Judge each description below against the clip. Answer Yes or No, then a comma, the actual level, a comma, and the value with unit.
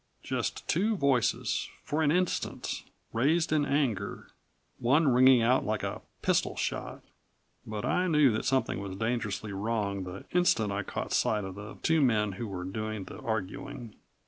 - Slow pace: No, average, 160 wpm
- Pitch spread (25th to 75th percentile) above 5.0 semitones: Yes, wide, 5.6 semitones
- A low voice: Yes, low, 115 Hz